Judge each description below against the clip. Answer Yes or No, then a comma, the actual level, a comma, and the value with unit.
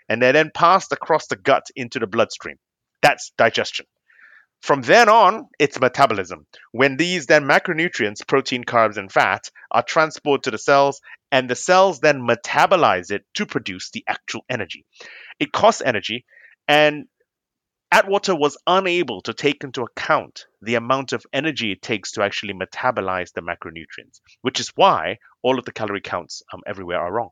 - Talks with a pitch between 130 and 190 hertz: Yes, medium, 140 Hz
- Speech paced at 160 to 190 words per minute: Yes, average, 165 wpm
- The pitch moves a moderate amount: Yes, average, 5.0 semitones